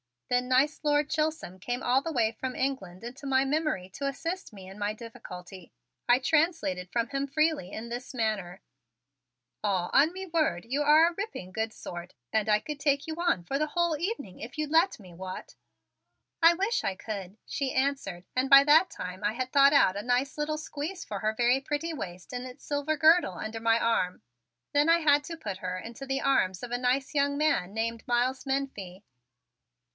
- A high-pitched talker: Yes, very high, 260 Hz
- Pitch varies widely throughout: Yes, wide, 6.0 semitones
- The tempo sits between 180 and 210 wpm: Yes, average, 200 wpm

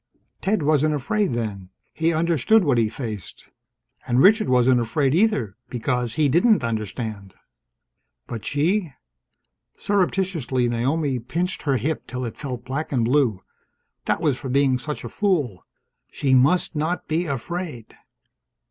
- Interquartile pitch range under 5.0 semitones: No, wide, 5.6 semitones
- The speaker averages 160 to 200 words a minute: No, average, 140 wpm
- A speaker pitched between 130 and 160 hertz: Yes, medium, 140 Hz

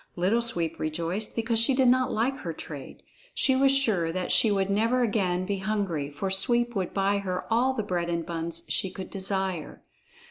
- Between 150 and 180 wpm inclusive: No, average, 190 wpm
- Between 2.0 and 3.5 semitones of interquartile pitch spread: No, average, 4.8 semitones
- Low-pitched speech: No, high, 195 Hz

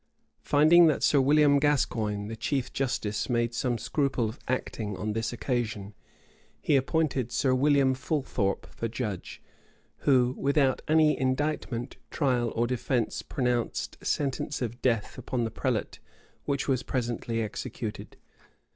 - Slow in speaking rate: Yes, slow, 130 wpm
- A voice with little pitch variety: No, average, 3.4 semitones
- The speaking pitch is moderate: No, low, 125 Hz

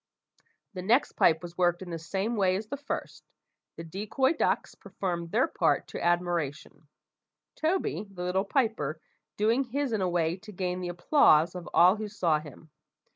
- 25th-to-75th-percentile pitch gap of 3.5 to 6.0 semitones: Yes, average, 4.2 semitones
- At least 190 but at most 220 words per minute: No, average, 175 wpm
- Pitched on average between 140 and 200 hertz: Yes, medium, 185 Hz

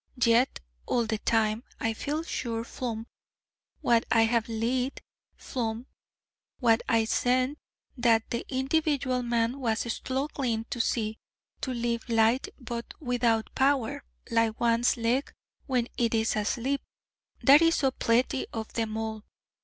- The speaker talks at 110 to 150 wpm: Yes, slow, 135 wpm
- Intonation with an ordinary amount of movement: No, narrow, 2.3 semitones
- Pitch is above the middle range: Yes, high, 235 Hz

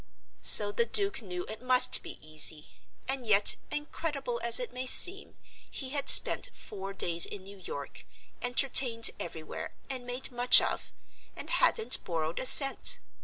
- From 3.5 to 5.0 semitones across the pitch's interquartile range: No, wide, 5.5 semitones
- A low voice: No, high, 240 Hz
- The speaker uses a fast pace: No, average, 155 wpm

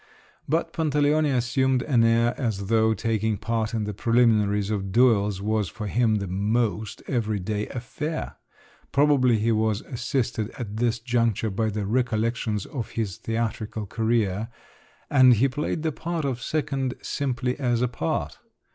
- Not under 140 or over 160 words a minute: Yes, average, 145 wpm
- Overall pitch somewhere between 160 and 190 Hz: No, low, 115 Hz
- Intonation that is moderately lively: Yes, average, 3.1 semitones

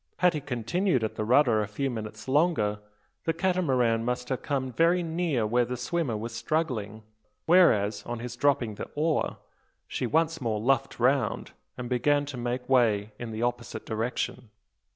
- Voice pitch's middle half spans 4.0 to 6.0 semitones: Yes, average, 4.7 semitones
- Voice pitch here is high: No, low, 125 Hz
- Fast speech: No, average, 170 wpm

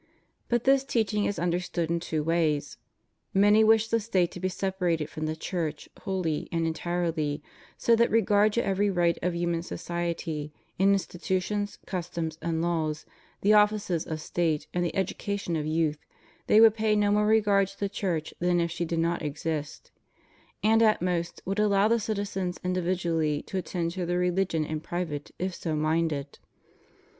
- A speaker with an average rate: Yes, average, 170 wpm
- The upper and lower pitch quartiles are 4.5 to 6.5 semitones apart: No, average, 3.7 semitones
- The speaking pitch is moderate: Yes, medium, 175 Hz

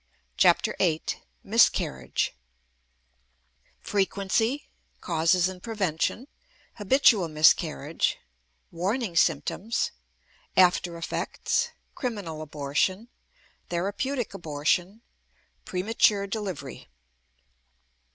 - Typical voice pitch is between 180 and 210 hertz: Yes, medium, 185 Hz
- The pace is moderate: No, slow, 65 wpm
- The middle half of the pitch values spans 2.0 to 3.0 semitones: No, average, 4.5 semitones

